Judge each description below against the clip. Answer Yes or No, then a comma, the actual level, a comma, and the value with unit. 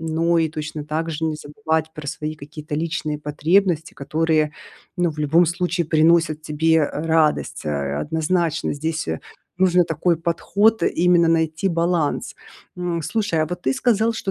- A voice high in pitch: No, medium, 160 Hz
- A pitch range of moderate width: No, narrow, 2.0 semitones